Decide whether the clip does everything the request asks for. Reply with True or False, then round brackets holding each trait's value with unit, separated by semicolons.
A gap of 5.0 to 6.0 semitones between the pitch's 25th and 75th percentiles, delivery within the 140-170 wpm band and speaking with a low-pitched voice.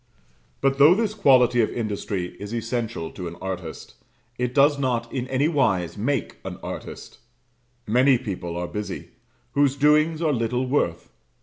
True (5.4 semitones; 145 wpm; 125 Hz)